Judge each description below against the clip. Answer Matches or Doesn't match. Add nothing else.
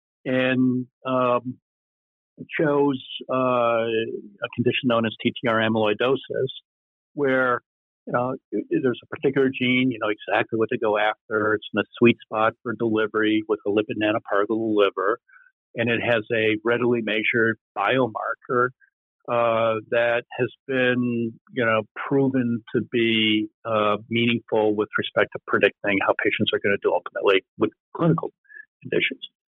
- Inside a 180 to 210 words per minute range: Doesn't match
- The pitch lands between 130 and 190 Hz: Doesn't match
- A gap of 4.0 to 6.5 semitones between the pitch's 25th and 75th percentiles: Doesn't match